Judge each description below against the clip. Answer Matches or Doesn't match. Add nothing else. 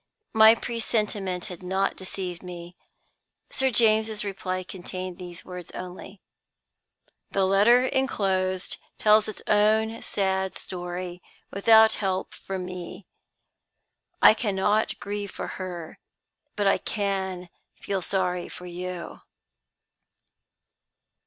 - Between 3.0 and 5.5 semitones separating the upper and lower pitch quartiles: Doesn't match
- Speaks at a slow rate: Matches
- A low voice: Doesn't match